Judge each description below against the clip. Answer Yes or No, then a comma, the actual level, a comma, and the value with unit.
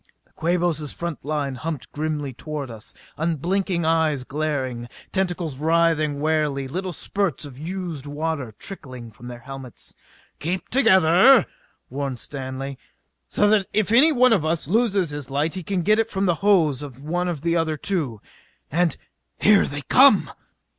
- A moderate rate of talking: Yes, average, 155 wpm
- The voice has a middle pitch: Yes, medium, 160 Hz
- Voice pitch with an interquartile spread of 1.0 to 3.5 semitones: No, average, 4.8 semitones